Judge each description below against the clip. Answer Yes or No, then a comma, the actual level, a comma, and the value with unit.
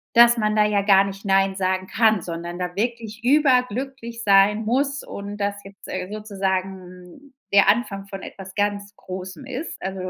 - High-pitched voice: Yes, high, 205 Hz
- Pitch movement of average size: Yes, average, 3.3 semitones